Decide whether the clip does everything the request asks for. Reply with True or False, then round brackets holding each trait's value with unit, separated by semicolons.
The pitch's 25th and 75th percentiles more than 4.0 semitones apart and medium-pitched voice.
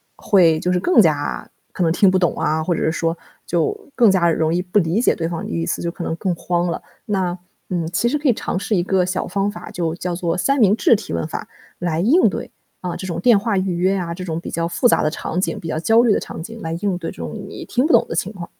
False (3.4 semitones; 180 Hz)